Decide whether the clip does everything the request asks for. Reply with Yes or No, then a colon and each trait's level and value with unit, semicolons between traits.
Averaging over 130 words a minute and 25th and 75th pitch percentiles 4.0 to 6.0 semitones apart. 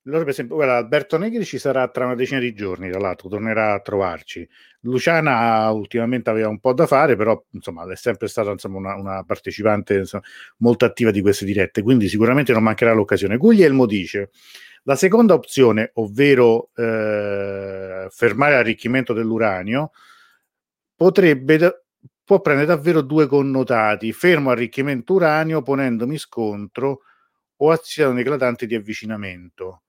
Yes: average, 140 wpm; average, 4.8 semitones